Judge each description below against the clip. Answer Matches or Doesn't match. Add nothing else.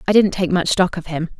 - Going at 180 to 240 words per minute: Doesn't match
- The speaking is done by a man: Doesn't match